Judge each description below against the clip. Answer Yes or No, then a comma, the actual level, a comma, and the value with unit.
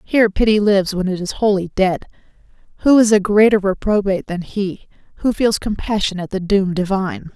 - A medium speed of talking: Yes, average, 180 wpm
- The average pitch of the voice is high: Yes, high, 200 Hz